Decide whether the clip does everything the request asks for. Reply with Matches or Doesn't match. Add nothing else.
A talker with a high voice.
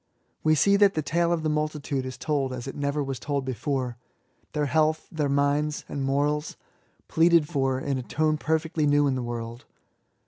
Doesn't match